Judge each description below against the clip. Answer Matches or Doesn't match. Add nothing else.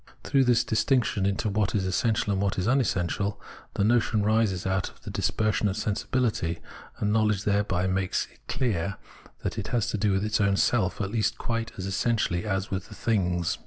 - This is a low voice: Matches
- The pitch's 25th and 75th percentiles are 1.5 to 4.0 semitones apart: Matches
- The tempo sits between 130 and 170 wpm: Doesn't match